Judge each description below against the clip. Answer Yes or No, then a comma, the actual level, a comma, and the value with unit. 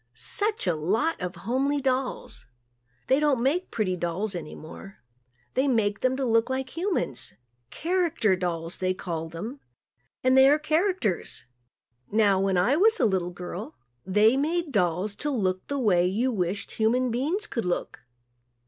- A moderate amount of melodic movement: No, wide, 7.1 semitones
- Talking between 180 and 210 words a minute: No, average, 155 wpm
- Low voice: No, high, 225 Hz